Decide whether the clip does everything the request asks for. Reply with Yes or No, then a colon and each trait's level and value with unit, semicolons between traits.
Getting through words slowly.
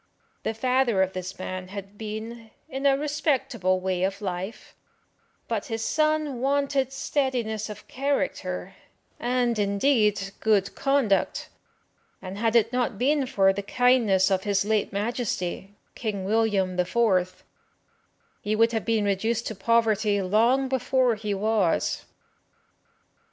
Yes: slow, 130 wpm